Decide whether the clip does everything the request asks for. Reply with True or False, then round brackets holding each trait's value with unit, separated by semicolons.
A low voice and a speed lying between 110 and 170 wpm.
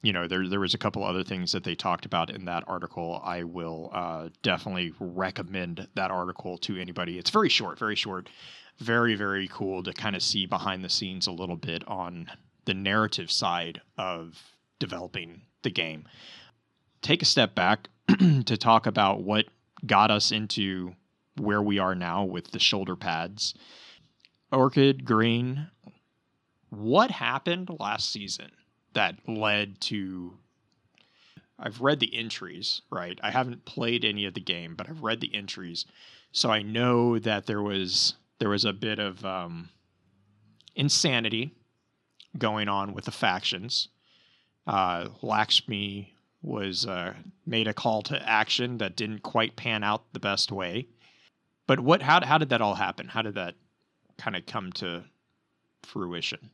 True (105 Hz; 155 wpm)